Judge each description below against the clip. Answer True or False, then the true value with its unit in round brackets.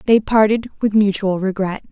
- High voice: True (205 Hz)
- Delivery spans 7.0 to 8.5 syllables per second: False (5.0 syllables/s)